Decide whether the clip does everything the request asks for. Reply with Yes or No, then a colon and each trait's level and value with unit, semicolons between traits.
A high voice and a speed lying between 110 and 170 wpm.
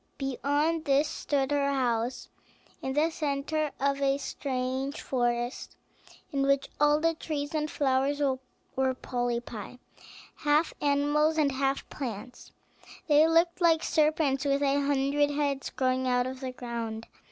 Yes: very high, 280 Hz; slow, 135 wpm